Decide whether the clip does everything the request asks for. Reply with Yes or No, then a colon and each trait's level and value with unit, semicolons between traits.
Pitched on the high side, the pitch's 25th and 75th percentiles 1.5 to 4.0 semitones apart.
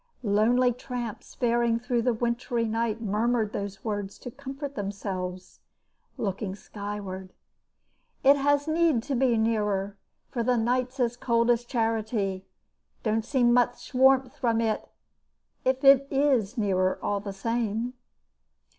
Yes: high, 230 Hz; average, 3.4 semitones